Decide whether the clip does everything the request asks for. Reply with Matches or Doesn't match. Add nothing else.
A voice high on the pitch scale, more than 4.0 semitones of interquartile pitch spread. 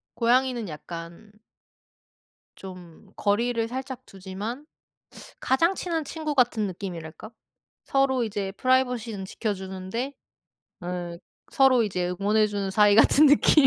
Matches